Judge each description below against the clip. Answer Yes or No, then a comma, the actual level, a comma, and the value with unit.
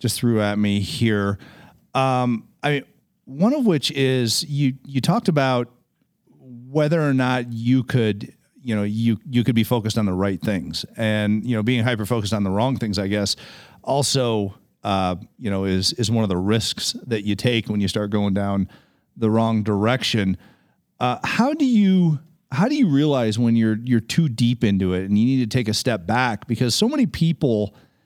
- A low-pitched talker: Yes, low, 120 Hz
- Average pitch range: Yes, average, 4.0 semitones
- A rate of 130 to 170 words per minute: No, average, 195 wpm